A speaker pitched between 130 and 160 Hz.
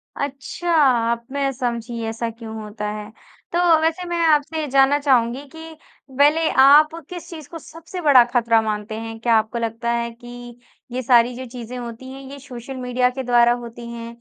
No: high, 245 Hz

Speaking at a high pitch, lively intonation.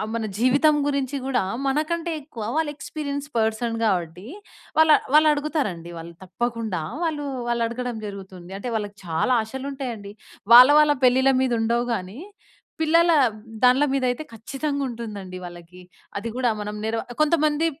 Yes: high, 245 Hz; wide, 5.7 semitones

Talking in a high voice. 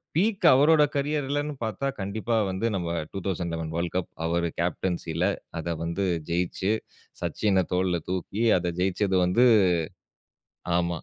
No: very low, 95 Hz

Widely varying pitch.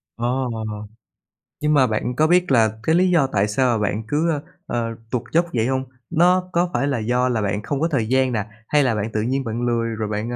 No: average, 4.8 semitones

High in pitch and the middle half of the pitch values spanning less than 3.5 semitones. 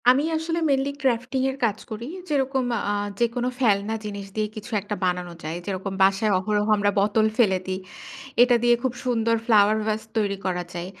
No: high, 215 Hz; average, 3.8 semitones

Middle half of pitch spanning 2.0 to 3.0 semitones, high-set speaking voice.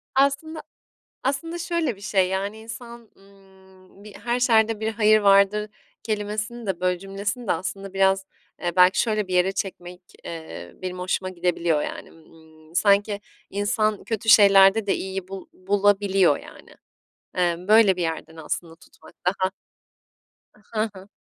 Yes: average, 2.7 semitones; high, 195 Hz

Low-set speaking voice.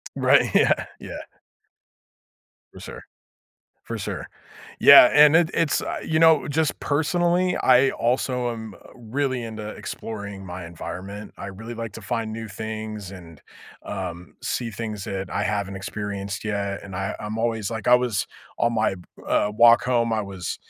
Yes: low, 110 Hz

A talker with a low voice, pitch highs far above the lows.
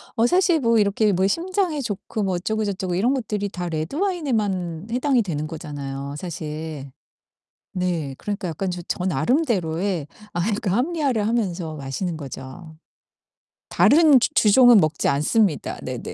No: high, 190 Hz; wide, 6.6 semitones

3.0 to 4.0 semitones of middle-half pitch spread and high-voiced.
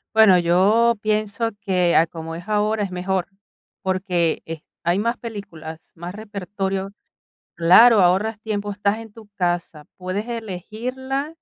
Yes: average, 3.6 semitones; high, 200 Hz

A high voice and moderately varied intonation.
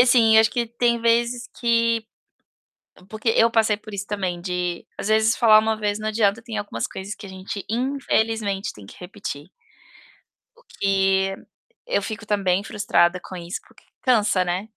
Yes: high, 215 Hz; average, 3.0 semitones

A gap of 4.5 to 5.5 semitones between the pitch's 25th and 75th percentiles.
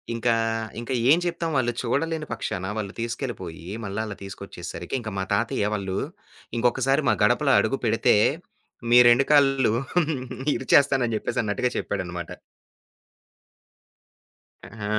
Yes: average, 5.1 semitones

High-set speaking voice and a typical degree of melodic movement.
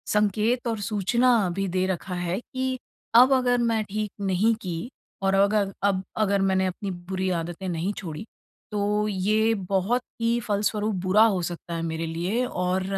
Yes: high, 200 Hz; average, 3.0 semitones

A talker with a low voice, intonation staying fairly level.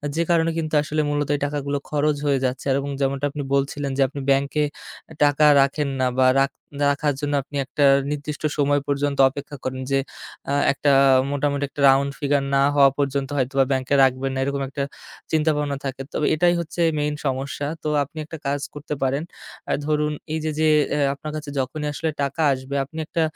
No: medium, 145 Hz; narrow, 1.5 semitones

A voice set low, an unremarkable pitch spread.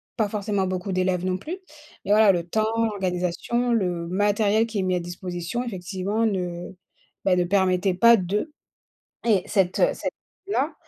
No: high, 190 Hz; average, 3.1 semitones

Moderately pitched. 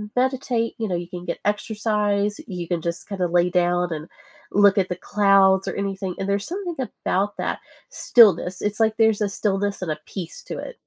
No: high, 200 Hz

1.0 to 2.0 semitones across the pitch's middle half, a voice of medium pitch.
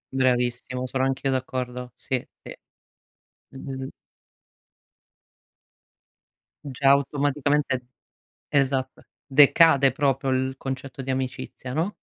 No: narrow, 1.3 semitones; low, 130 Hz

